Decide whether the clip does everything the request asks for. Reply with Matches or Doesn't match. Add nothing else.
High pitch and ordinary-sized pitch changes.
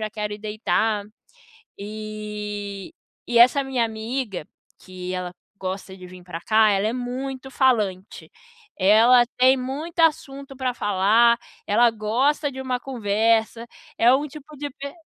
Matches